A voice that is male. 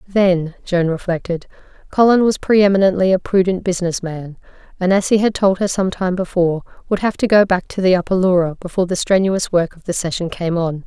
No: female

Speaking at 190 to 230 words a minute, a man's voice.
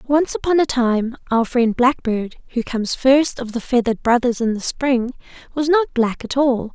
No: average, 195 wpm; female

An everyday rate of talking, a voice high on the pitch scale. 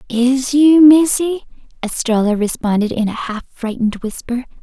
No: slow, 130 wpm; very high, 250 Hz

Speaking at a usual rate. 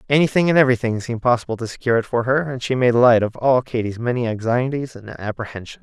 No: fast, 215 wpm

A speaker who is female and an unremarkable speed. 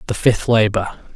No: male; average, 155 wpm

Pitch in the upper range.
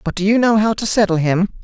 Yes: high, 200 Hz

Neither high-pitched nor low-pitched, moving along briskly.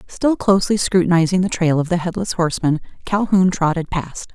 No: medium, 180 Hz; average, 165 wpm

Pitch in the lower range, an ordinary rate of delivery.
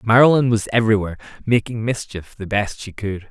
Yes: low, 110 Hz; average, 165 wpm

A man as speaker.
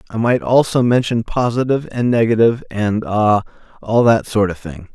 Yes: male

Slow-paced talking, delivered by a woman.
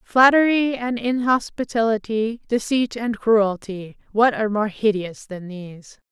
Yes: slow, 110 wpm; female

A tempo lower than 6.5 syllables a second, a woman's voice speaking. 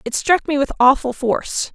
Yes: 5.1 syllables/s; female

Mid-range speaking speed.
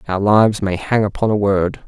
No: fast, 225 wpm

